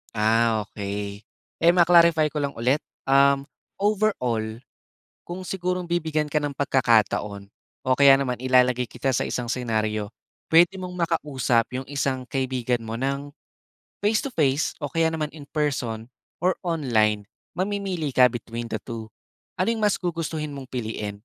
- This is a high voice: No, low, 135 Hz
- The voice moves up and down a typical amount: No, wide, 6.1 semitones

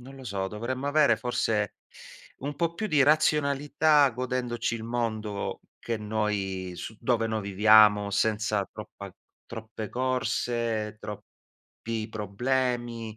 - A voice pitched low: Yes, low, 115 Hz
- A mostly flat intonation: No, average, 3.4 semitones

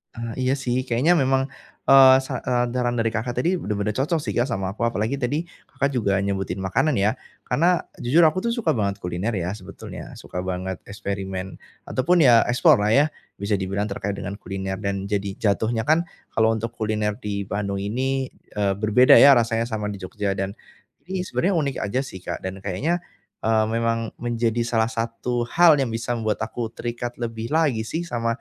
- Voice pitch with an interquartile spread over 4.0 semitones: Yes, average, 4.4 semitones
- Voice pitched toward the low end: Yes, low, 115 Hz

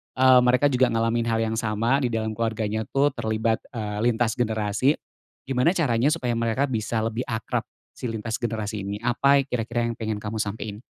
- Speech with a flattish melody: Yes, narrow, 2.1 semitones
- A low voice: Yes, low, 115 Hz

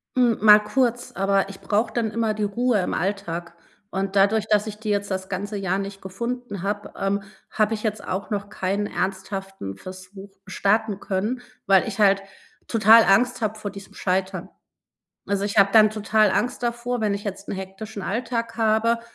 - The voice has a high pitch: Yes, high, 205 Hz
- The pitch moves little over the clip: Yes, narrow, 2.1 semitones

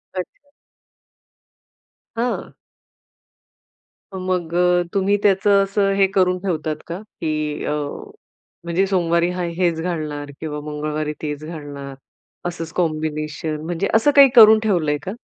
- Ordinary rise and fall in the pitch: Yes, average, 4.0 semitones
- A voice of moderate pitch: Yes, medium, 170 Hz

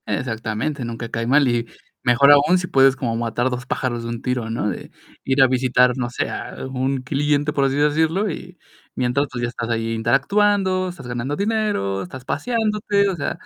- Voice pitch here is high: No, low, 130 Hz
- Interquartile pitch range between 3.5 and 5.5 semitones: Yes, average, 4.4 semitones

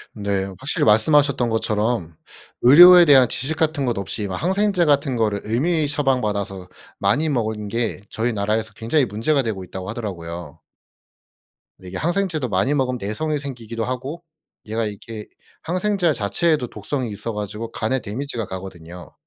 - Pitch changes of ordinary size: No, wide, 5.9 semitones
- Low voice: Yes, low, 115 Hz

